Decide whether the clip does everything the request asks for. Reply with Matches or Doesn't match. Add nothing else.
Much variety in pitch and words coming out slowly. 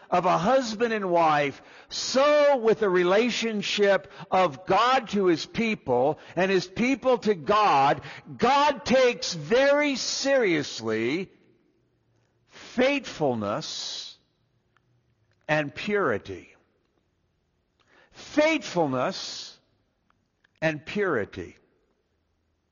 Matches